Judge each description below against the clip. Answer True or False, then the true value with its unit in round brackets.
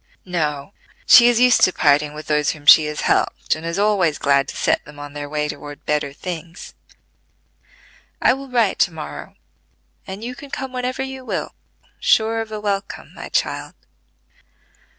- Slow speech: False (170 wpm)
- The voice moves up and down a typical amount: False (7.2 semitones)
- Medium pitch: True (175 Hz)